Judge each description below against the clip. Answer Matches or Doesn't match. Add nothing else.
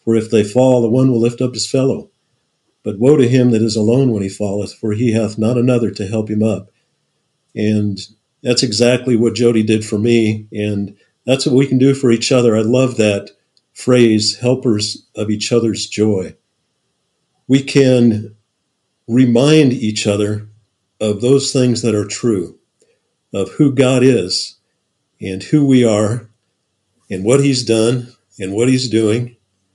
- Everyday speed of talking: Matches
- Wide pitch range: Doesn't match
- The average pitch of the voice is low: Matches